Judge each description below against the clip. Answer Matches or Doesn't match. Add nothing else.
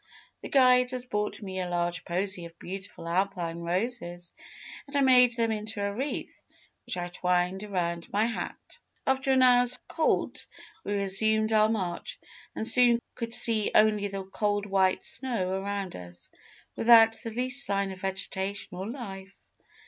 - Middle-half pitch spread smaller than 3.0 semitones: Doesn't match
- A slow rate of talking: Doesn't match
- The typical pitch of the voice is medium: Doesn't match